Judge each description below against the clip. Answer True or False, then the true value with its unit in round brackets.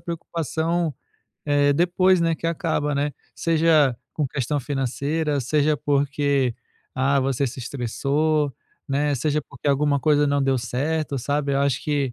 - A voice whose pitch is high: False (145 Hz)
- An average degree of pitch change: False (2.0 semitones)